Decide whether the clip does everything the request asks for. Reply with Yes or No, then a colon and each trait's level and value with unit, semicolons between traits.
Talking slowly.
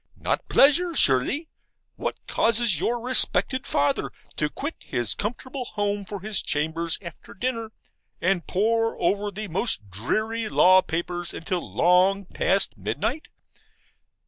Yes: slow, 125 wpm